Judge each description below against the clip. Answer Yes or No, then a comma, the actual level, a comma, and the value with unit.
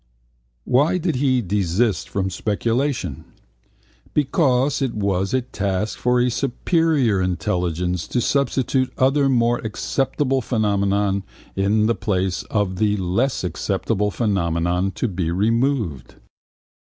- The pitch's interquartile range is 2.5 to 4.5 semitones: No, wide, 5.4 semitones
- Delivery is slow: Yes, slow, 115 wpm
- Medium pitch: No, low, 105 Hz